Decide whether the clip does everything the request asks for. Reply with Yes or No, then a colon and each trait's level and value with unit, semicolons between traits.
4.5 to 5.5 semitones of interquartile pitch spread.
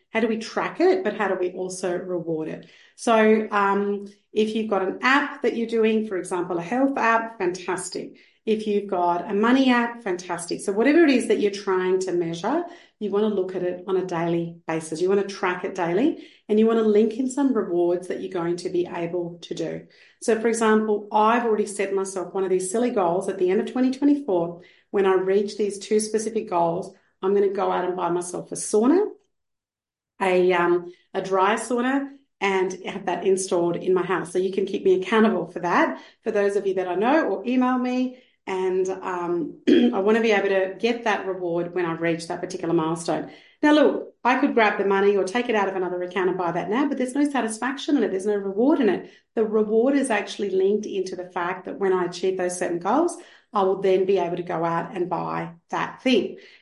No: average, 3.9 semitones